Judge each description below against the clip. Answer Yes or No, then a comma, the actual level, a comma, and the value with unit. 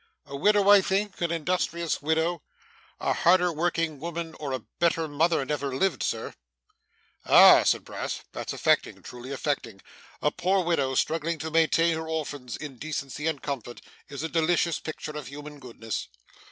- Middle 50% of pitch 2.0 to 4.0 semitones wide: Yes, average, 3.2 semitones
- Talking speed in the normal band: Yes, average, 160 wpm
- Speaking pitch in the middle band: Yes, medium, 160 Hz